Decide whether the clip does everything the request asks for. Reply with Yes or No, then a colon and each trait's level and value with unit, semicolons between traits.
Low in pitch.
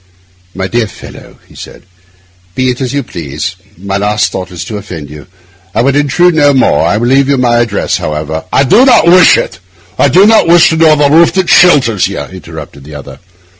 Yes: low, 120 Hz